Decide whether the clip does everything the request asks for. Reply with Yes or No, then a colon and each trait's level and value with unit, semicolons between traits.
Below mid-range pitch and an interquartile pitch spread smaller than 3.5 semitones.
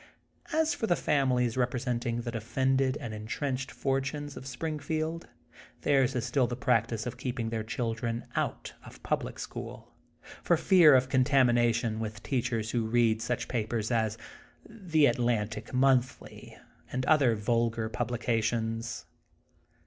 Yes: low, 120 Hz; average, 2.8 semitones